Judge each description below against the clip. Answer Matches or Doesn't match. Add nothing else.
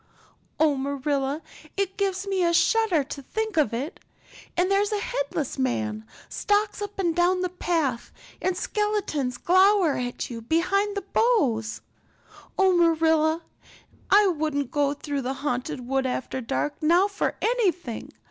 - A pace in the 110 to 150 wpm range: Matches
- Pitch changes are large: Matches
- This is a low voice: Doesn't match